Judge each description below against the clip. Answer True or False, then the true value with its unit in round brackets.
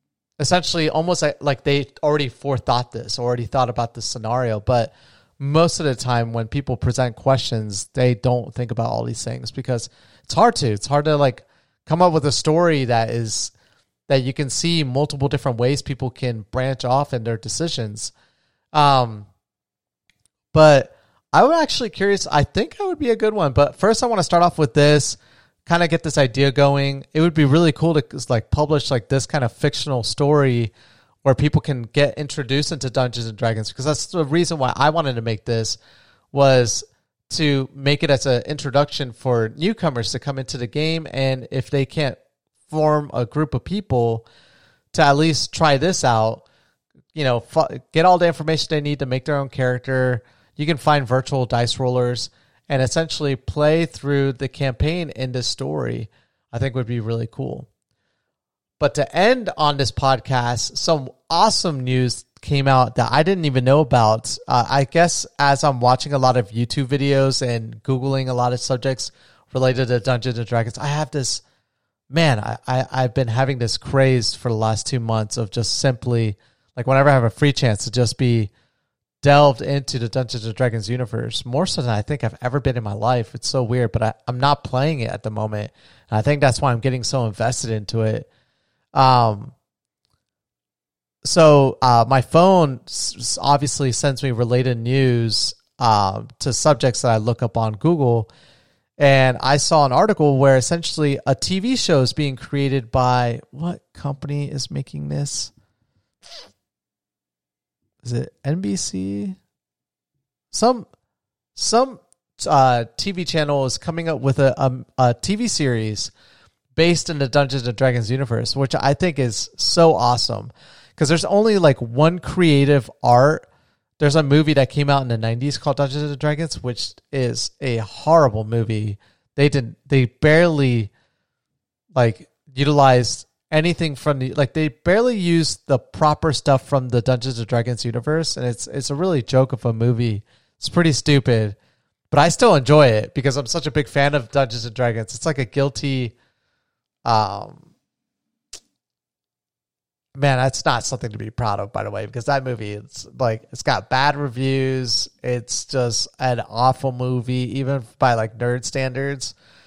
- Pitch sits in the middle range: False (130 Hz)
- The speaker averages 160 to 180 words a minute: True (175 wpm)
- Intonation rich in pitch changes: False (3.4 semitones)